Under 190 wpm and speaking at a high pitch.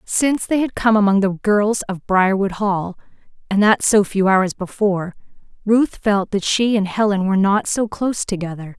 Yes: average, 170 wpm; high, 200 Hz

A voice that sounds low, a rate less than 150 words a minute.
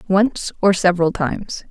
No: high, 190 Hz; average, 140 wpm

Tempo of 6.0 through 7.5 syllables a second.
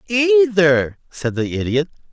No: 3.7 syllables/s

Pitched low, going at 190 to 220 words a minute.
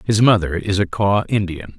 Yes: very low, 95 Hz; average, 200 wpm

